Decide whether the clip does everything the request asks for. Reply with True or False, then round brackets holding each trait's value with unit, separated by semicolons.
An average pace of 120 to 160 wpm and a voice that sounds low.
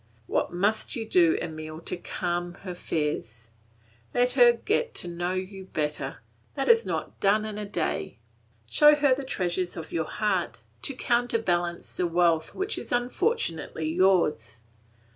False (150 wpm; 185 Hz)